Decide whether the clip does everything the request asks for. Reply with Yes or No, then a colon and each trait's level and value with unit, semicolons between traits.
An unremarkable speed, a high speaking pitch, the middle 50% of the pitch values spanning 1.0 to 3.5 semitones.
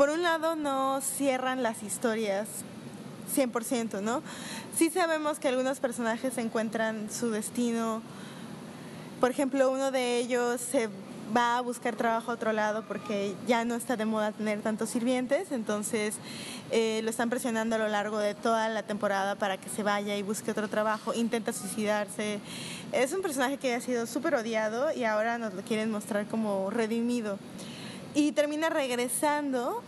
Yes: average, 160 wpm; high, 230 Hz; average, 3.1 semitones